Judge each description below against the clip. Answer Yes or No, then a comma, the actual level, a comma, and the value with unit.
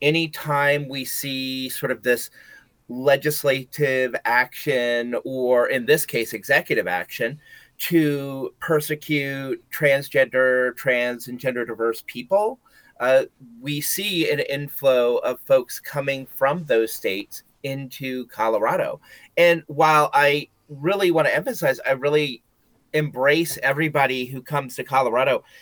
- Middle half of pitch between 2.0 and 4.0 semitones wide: Yes, average, 3.0 semitones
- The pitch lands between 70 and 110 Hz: No, medium, 140 Hz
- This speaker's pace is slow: Yes, slow, 115 wpm